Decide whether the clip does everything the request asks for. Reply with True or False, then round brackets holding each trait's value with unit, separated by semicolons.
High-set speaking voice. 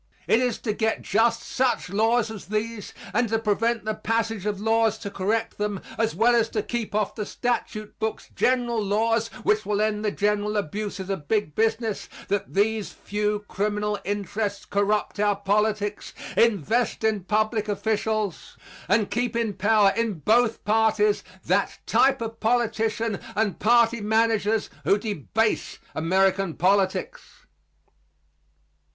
True (215 Hz)